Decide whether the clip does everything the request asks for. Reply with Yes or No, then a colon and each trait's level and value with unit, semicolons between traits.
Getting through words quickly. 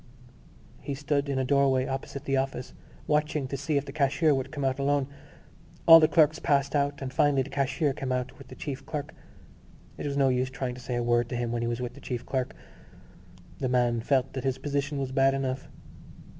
Yes: fast, 220 wpm